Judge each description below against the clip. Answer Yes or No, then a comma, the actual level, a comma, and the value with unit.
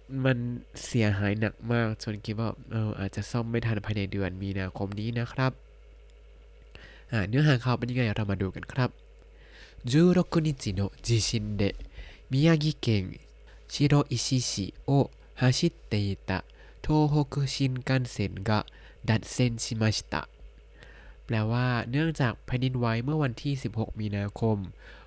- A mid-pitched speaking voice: No, low, 115 Hz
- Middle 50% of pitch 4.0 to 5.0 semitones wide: Yes, average, 4.3 semitones